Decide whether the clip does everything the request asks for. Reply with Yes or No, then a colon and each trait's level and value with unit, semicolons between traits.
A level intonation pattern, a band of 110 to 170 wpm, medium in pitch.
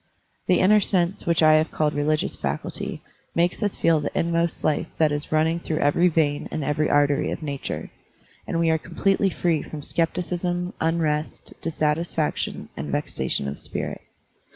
Yes: narrow, 2.2 semitones; average, 160 wpm; medium, 160 Hz